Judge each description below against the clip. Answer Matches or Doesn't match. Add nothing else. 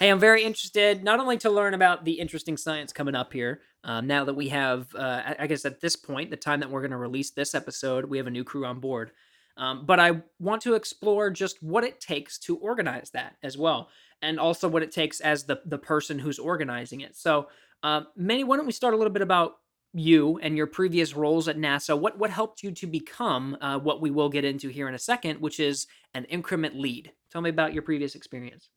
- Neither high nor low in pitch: Matches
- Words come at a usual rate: Doesn't match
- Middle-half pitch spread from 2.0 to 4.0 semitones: Doesn't match